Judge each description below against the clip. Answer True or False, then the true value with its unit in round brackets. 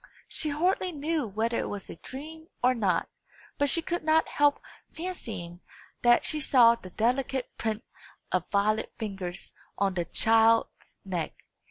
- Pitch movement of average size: False (6.8 semitones)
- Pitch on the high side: True (235 Hz)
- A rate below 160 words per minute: True (150 wpm)